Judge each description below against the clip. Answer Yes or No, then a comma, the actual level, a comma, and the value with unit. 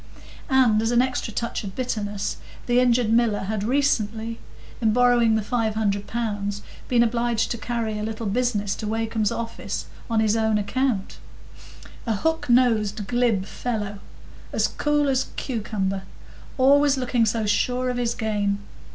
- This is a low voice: No, high, 225 Hz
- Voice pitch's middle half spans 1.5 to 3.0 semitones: Yes, average, 2.7 semitones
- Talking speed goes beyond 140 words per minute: Yes, average, 150 wpm